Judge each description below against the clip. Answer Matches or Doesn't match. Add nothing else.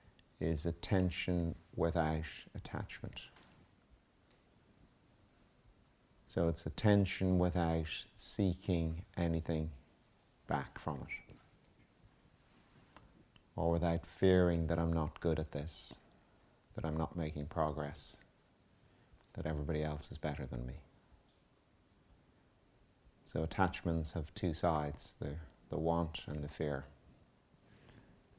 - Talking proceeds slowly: Matches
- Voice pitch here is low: Matches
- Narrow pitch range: Matches